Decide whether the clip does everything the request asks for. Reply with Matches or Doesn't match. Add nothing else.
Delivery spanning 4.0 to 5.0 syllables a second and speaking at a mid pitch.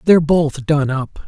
Matches